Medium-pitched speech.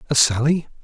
Yes: medium, 145 Hz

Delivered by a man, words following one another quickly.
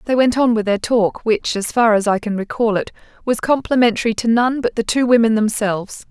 No: female; fast, 225 wpm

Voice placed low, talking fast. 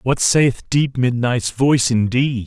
No: low, 125 Hz; average, 145 wpm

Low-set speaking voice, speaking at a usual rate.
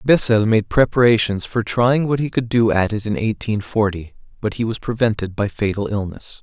Yes: low, 110 Hz; average, 195 wpm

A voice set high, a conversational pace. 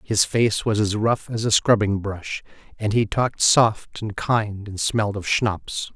No: low, 105 Hz; average, 190 wpm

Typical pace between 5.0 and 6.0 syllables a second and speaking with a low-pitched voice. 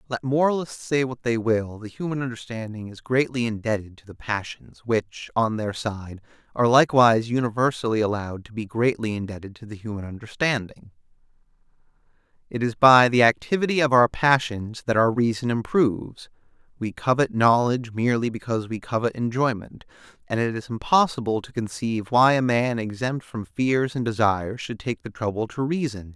Yes: 5.4 syllables/s; low, 120 Hz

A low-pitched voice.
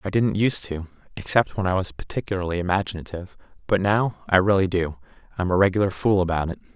Yes: very low, 95 Hz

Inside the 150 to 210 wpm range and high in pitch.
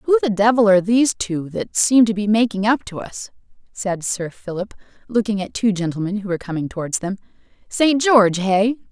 Yes: average, 195 wpm; high, 210 Hz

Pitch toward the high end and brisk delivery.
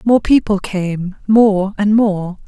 No: high, 200 Hz; slow, 120 wpm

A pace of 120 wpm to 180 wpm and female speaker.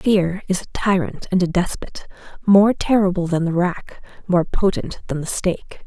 Yes: average, 175 wpm; female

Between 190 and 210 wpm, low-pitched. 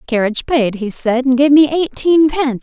No: fast, 205 wpm; very high, 265 Hz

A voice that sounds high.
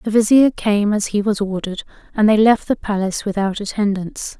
Yes: high, 205 Hz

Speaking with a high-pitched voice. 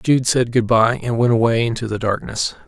No: low, 115 Hz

